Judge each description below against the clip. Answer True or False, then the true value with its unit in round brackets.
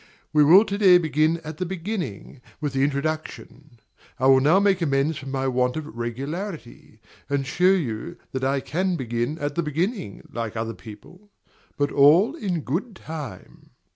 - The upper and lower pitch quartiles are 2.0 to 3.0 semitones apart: False (5.1 semitones)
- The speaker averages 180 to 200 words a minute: False (170 wpm)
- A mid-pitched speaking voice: True (150 Hz)